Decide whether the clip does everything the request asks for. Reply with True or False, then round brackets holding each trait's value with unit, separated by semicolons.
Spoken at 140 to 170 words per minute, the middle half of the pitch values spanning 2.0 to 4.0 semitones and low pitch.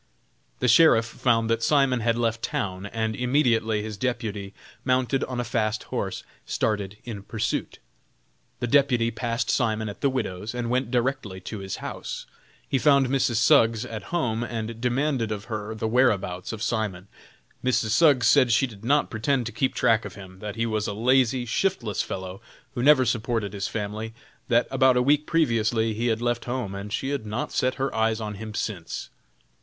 False (180 wpm; 2.9 semitones; 115 Hz)